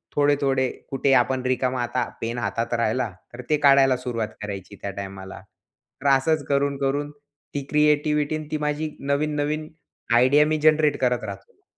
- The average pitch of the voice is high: No, low, 135 Hz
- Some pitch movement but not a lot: Yes, average, 3.3 semitones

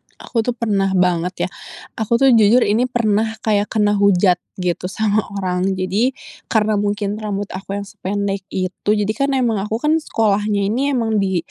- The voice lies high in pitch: Yes, high, 205 Hz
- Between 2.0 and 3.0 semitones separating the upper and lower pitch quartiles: Yes, narrow, 2.4 semitones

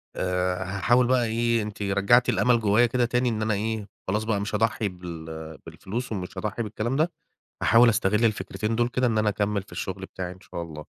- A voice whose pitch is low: Yes, low, 105 Hz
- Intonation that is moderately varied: Yes, average, 3.6 semitones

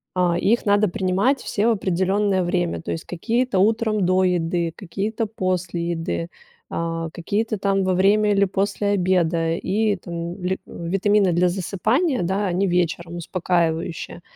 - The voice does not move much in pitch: No, average, 3.0 semitones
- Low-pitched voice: No, medium, 185 Hz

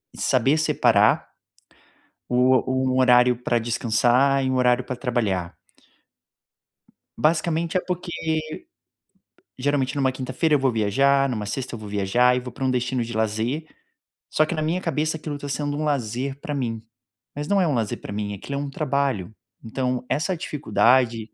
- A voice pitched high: No, low, 130 Hz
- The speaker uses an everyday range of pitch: Yes, average, 3.3 semitones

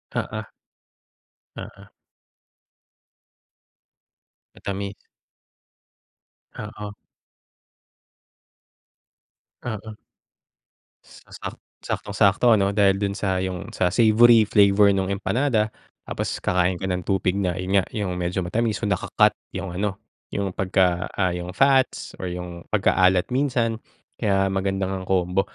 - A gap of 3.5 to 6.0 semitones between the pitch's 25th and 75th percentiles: No, narrow, 2.4 semitones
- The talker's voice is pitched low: Yes, very low, 95 Hz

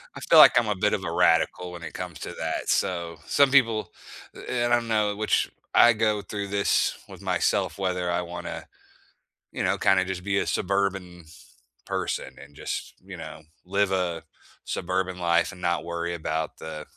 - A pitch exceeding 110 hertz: No, very low, 95 Hz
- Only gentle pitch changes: No, average, 3.0 semitones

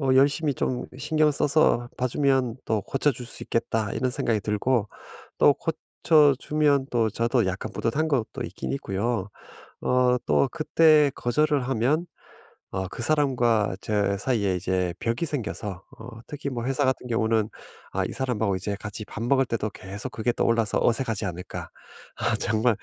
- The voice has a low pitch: Yes, low, 120 Hz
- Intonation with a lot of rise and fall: No, average, 4.3 semitones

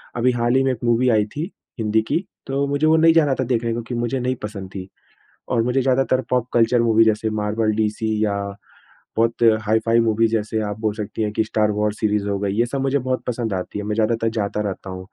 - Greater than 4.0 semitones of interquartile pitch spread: No, average, 2.8 semitones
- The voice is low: Yes, low, 115 Hz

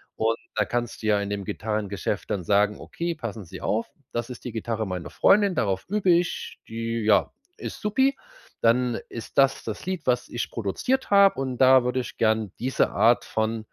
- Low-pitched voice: Yes, low, 115 Hz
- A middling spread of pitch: Yes, average, 3.7 semitones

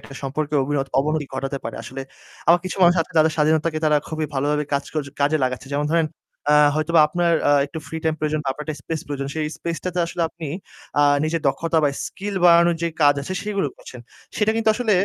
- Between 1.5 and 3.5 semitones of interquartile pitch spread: Yes, average, 2.7 semitones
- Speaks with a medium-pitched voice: Yes, medium, 155 Hz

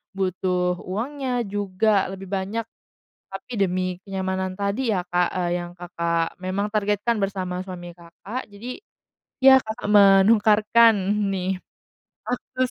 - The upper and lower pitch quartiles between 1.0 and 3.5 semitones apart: Yes, average, 2.9 semitones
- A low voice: No, high, 195 Hz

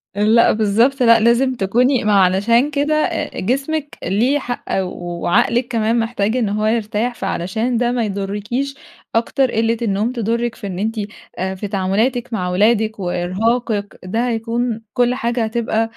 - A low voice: No, high, 225 Hz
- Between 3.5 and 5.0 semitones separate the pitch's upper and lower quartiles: No, average, 3.1 semitones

